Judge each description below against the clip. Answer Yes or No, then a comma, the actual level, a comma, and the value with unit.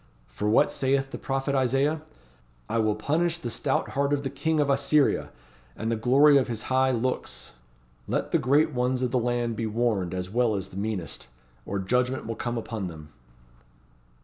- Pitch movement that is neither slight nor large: Yes, average, 3.7 semitones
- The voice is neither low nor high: No, low, 125 Hz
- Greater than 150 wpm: Yes, average, 185 wpm